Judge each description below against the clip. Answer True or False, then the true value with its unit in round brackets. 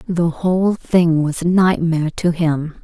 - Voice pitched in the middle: True (170 Hz)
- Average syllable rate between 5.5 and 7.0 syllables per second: False (4.1 syllables/s)